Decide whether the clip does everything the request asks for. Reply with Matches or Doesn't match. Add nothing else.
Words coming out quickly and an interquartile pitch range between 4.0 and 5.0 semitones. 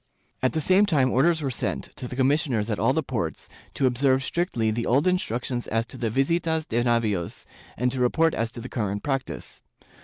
Matches